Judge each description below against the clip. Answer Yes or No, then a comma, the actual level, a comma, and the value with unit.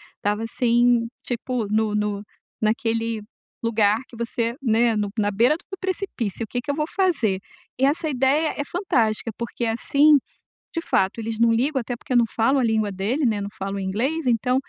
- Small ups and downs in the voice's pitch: No, average, 3.6 semitones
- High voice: Yes, high, 230 Hz